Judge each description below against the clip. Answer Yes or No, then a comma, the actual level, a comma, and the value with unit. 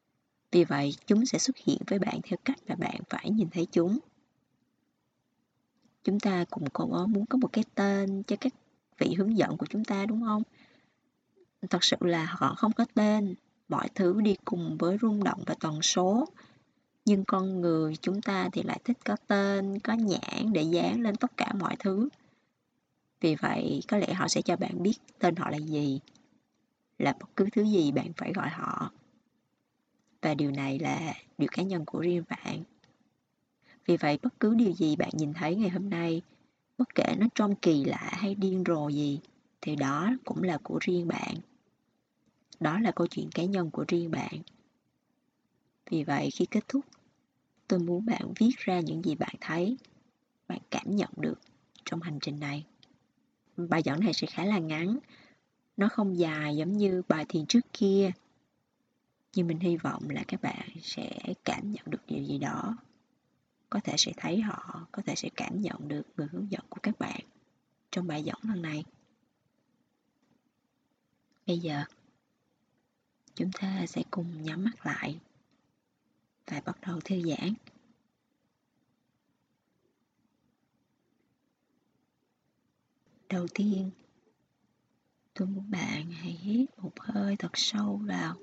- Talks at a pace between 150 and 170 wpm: Yes, slow, 165 wpm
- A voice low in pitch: No, high, 195 Hz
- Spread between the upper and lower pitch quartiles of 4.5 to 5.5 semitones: Yes, average, 4.8 semitones